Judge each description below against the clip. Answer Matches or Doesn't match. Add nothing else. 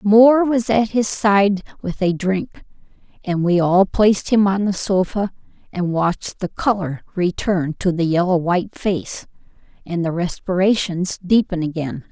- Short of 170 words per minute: Matches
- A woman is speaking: Matches